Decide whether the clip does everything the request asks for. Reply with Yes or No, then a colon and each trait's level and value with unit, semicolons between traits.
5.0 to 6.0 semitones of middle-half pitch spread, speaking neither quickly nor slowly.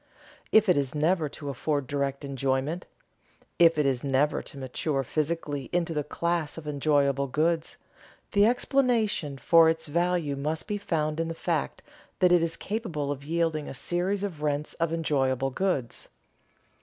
No: average, 3.4 semitones; average, 160 wpm